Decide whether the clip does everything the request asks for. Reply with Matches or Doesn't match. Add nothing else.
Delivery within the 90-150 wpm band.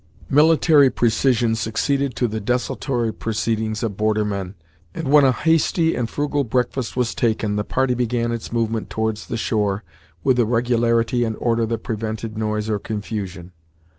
Doesn't match